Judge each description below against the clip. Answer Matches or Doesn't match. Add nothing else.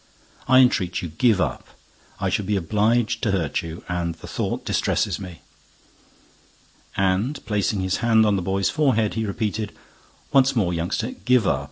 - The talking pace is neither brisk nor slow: Matches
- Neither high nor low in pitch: Doesn't match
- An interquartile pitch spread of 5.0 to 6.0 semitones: Doesn't match